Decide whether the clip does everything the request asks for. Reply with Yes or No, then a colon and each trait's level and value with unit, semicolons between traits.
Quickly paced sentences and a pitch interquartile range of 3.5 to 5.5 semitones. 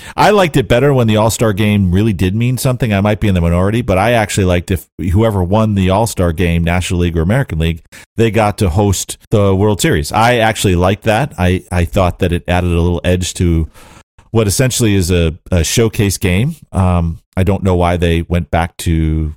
Yes: fast, 215 wpm; average, 4.0 semitones